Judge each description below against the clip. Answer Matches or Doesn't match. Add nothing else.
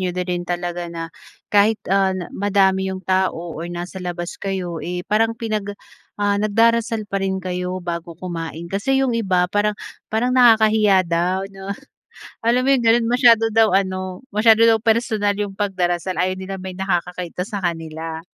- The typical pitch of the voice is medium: Doesn't match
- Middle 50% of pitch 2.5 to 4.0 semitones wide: Matches